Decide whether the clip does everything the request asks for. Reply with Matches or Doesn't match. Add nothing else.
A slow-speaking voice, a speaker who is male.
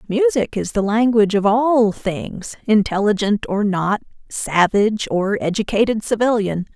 Doesn't match